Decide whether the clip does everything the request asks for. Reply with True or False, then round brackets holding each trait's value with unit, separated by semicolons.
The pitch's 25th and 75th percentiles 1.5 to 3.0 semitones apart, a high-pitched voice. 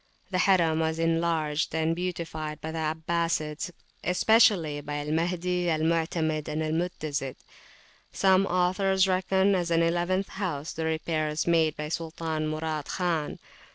False (2.4 semitones; 165 Hz)